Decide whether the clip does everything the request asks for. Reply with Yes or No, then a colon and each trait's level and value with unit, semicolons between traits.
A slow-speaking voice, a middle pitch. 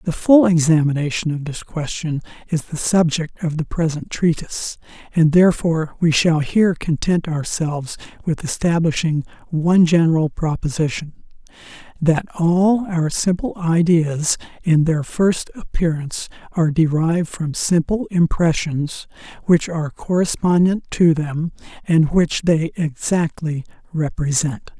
Yes: slow, 120 wpm; medium, 165 Hz